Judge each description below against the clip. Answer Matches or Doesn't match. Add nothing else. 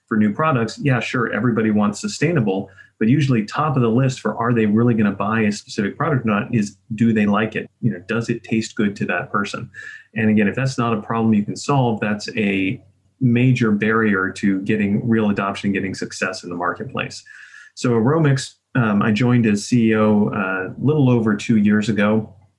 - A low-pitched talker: Matches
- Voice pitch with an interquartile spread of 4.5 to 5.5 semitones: Doesn't match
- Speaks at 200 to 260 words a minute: Matches